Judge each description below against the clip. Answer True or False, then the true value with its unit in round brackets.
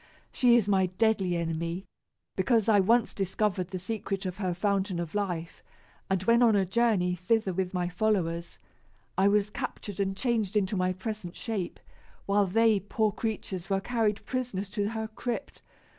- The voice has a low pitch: False (200 Hz)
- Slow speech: False (165 wpm)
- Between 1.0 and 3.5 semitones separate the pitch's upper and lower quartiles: True (3.1 semitones)